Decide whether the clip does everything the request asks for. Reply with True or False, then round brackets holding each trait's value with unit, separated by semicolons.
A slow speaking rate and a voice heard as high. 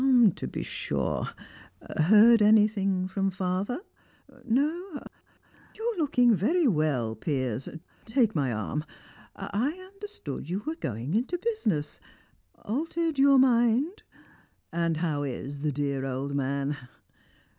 True (115 wpm; 200 Hz)